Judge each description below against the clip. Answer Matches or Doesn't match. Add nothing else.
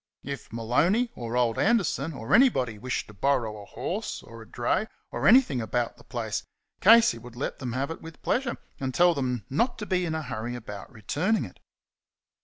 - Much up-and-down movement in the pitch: Matches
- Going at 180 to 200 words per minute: Matches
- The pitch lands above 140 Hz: Doesn't match